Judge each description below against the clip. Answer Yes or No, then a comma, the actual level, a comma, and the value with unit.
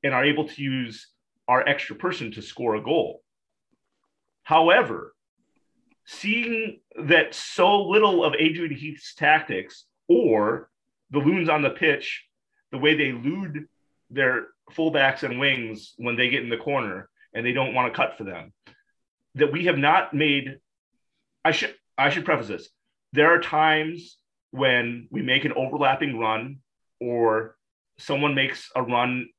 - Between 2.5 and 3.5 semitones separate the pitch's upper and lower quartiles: No, average, 4.5 semitones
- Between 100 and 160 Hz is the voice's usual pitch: Yes, medium, 140 Hz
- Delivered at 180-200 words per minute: No, average, 150 wpm